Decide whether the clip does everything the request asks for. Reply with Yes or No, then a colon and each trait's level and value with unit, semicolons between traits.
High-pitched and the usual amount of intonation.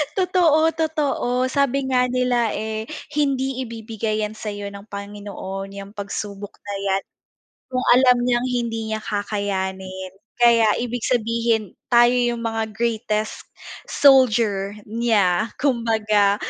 Yes: high, 225 Hz; average, 3.5 semitones